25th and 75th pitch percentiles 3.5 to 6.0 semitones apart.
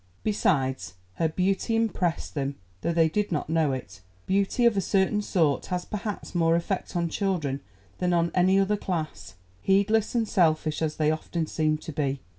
Yes: average, 4.1 semitones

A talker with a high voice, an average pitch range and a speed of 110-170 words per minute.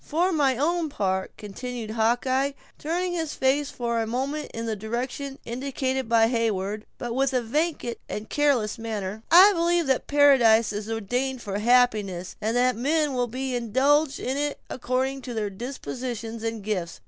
Yes: high, 245 Hz; average, 3.8 semitones; average, 165 wpm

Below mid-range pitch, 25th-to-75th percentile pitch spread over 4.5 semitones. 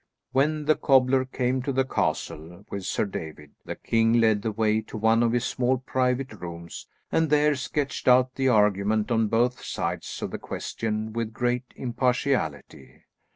No: low, 120 Hz; average, 3.4 semitones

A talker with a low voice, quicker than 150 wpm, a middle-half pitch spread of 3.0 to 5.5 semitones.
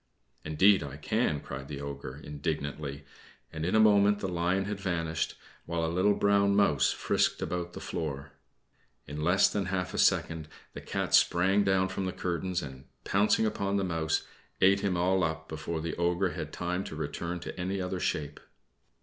Yes: very low, 90 Hz; average, 180 wpm; average, 3.7 semitones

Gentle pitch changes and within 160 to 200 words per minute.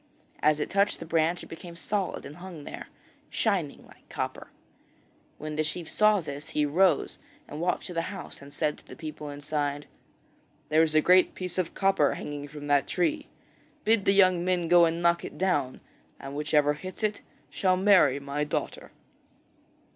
No: average, 3.9 semitones; average, 180 wpm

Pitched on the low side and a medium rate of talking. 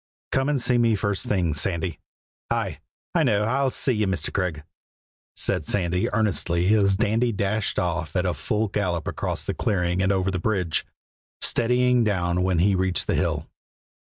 Yes: very low, 95 Hz; average, 170 wpm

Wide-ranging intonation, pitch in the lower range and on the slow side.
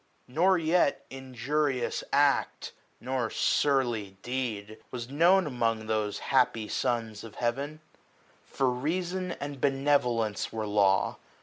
No: average, 4.3 semitones; low, 130 Hz; slow, 115 wpm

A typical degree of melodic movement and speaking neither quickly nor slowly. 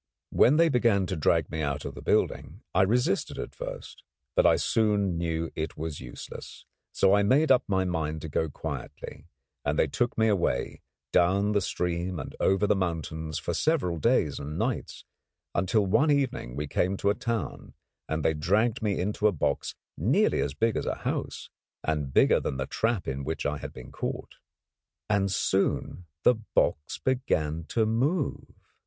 No: wide, 6.1 semitones; average, 175 wpm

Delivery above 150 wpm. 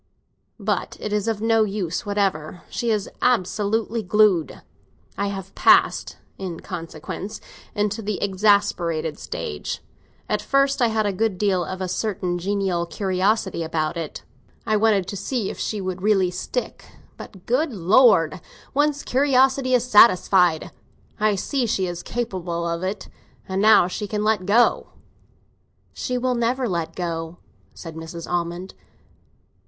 No: average, 145 wpm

